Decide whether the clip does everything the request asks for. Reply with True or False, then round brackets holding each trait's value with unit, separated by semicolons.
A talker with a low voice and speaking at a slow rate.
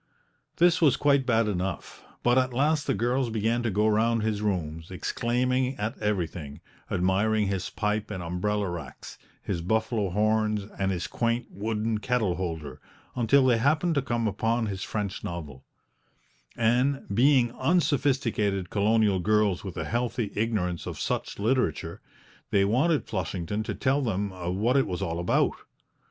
False (110 Hz; 150 wpm)